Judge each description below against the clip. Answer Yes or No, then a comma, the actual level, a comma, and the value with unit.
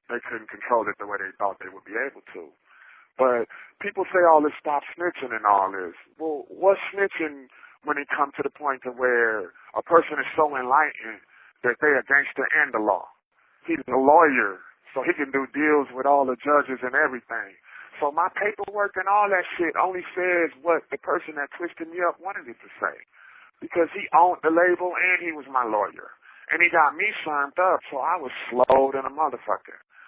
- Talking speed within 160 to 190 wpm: No, fast, 205 wpm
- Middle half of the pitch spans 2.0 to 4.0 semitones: No, average, 4.9 semitones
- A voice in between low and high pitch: Yes, medium, 160 Hz